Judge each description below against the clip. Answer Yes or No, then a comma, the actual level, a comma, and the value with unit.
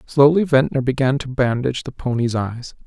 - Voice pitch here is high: No, low, 130 Hz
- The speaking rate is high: No, average, 170 wpm